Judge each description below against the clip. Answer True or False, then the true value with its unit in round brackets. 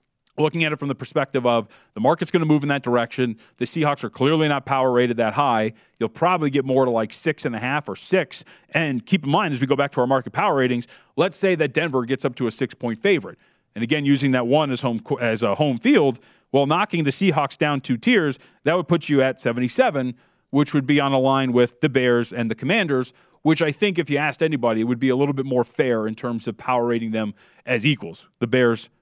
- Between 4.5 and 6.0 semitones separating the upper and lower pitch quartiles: False (3.8 semitones)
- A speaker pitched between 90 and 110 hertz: False (135 Hz)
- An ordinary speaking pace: False (250 wpm)